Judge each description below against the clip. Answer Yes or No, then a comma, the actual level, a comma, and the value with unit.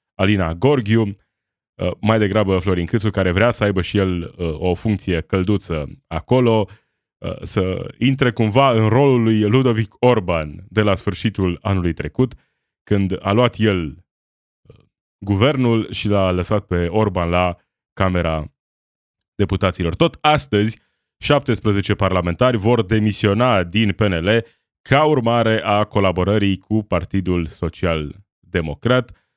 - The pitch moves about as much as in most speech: Yes, average, 3.8 semitones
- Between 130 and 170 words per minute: No, average, 120 wpm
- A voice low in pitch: Yes, low, 100 Hz